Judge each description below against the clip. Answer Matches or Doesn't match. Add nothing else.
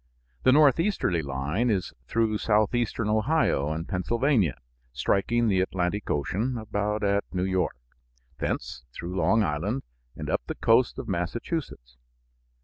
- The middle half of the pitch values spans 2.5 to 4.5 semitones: Doesn't match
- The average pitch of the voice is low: Matches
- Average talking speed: Doesn't match